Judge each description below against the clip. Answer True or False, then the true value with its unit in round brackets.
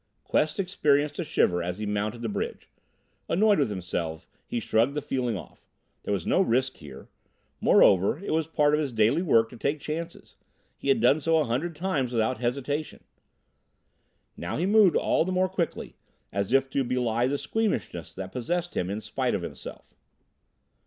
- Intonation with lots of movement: True (6.5 semitones)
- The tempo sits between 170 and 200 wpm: True (180 wpm)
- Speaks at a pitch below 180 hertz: True (135 Hz)